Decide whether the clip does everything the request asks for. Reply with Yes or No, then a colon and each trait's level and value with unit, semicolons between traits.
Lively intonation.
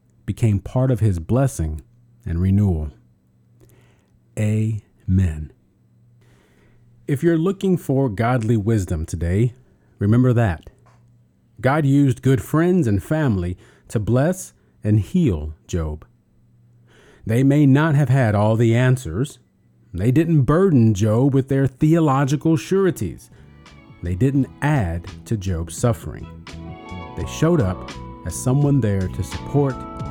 Yes: wide, 6.8 semitones